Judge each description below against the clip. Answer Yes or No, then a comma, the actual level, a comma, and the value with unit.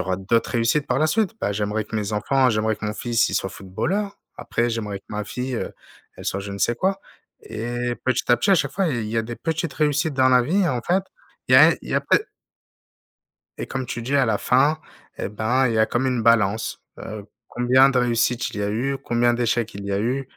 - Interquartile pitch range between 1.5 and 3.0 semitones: No, average, 3.7 semitones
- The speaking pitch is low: Yes, low, 120 Hz